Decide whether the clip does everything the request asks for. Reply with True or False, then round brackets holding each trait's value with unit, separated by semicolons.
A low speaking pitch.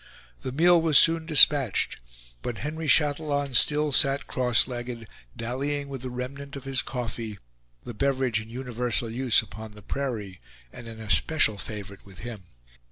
True (125 Hz)